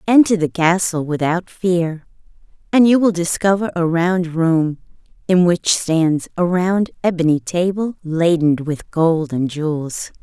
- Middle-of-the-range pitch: Yes, medium, 170 Hz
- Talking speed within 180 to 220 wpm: No, average, 140 wpm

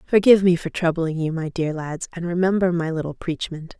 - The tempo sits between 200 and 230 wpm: Yes, fast, 205 wpm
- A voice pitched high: No, medium, 170 Hz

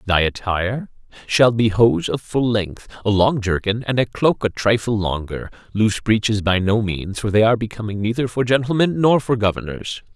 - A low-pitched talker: Yes, low, 110 Hz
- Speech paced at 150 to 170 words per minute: No, average, 190 wpm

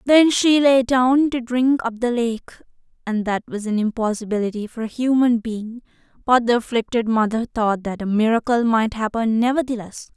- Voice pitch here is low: No, high, 235 Hz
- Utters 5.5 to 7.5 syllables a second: No, 5.0 syllables/s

